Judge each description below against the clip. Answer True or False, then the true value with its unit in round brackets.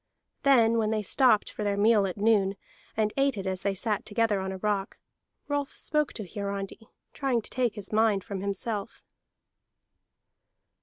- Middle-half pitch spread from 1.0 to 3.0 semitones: True (2.5 semitones)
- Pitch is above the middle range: True (210 Hz)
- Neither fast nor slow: True (165 wpm)